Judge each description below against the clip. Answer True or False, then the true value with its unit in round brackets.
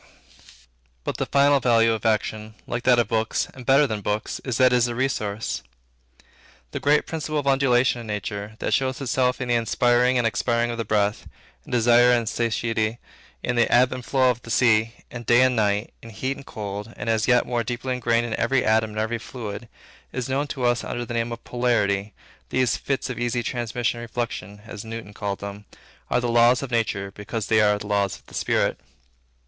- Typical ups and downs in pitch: False (2.3 semitones)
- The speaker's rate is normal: False (210 wpm)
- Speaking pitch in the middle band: False (120 Hz)